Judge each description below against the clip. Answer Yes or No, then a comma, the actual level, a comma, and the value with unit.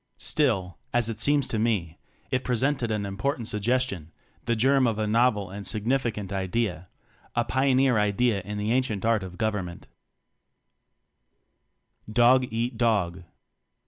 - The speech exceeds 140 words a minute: No, slow, 135 wpm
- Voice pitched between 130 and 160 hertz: No, low, 110 Hz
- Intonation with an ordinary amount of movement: Yes, average, 3.8 semitones